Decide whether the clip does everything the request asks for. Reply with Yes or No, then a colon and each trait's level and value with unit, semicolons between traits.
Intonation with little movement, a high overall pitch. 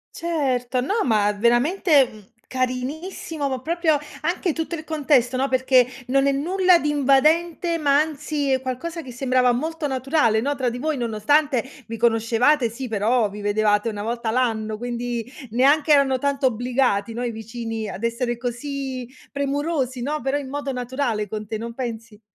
No: average, 3.8 semitones; very high, 255 Hz